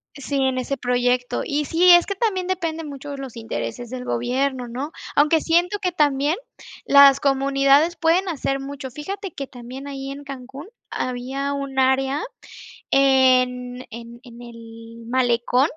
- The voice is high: Yes, very high, 275 Hz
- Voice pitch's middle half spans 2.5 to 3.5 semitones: Yes, average, 2.8 semitones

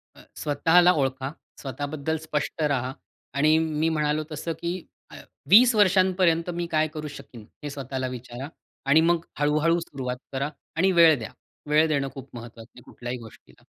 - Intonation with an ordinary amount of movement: Yes, average, 3.5 semitones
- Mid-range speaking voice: Yes, medium, 150 Hz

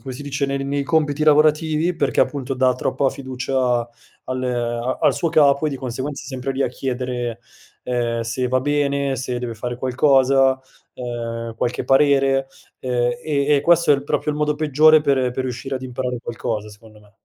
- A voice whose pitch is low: Yes, low, 130 Hz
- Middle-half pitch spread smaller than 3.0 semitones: Yes, narrow, 2.5 semitones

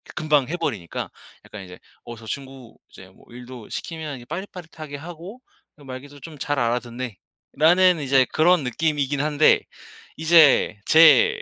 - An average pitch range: Yes, average, 4.6 semitones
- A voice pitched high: No, medium, 145 Hz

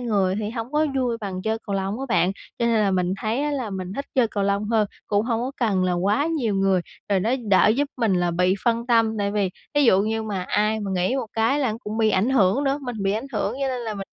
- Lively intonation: No, average, 3.5 semitones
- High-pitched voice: Yes, high, 215 Hz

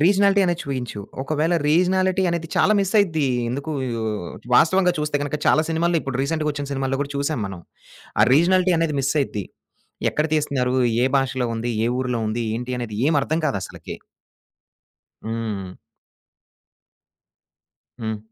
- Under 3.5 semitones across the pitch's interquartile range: No, average, 4.9 semitones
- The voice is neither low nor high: Yes, medium, 145 Hz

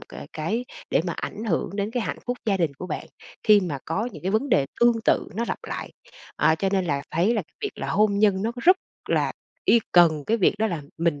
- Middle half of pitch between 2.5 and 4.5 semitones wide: No, average, 5.1 semitones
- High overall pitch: Yes, high, 200 Hz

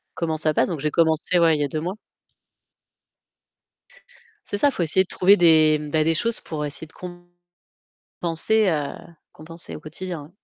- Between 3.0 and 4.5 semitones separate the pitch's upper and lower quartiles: No, narrow, 2.4 semitones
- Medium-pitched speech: Yes, medium, 160 Hz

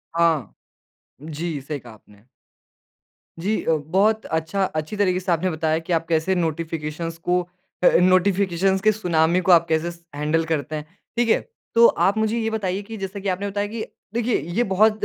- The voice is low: No, medium, 180 Hz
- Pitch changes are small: No, average, 4.0 semitones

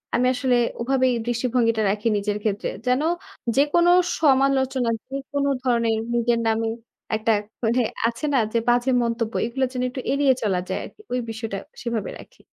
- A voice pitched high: Yes, high, 240 Hz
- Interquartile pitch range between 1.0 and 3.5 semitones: Yes, average, 2.7 semitones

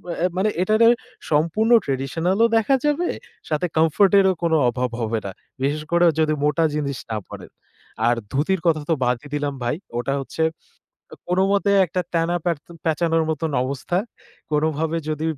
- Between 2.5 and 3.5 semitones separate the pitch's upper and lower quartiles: No, average, 3.9 semitones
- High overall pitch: No, medium, 160 Hz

